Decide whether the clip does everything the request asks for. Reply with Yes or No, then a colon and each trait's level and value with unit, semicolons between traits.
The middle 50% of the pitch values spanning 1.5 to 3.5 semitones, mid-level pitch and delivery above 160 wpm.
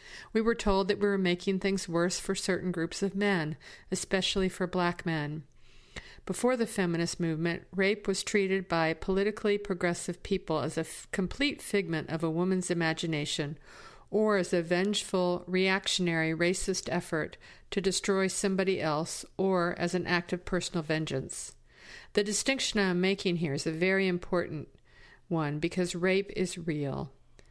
No: average, 2.7 semitones; medium, 180 Hz; average, 155 wpm